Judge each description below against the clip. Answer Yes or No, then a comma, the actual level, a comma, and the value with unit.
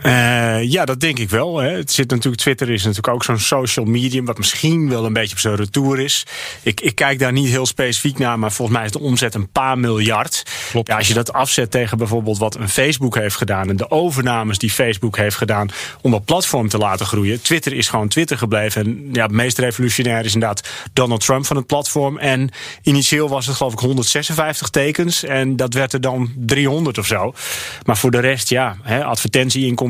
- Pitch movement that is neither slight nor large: Yes, average, 3.4 semitones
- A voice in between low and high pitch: No, low, 125 Hz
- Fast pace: Yes, fast, 215 wpm